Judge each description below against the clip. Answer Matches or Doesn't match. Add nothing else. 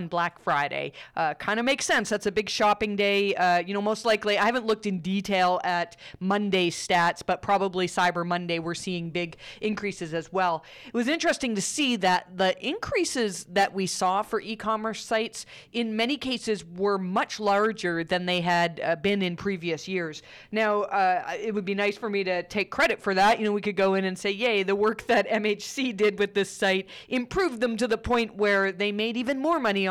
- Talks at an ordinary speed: Doesn't match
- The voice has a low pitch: Doesn't match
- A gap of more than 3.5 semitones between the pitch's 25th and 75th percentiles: Doesn't match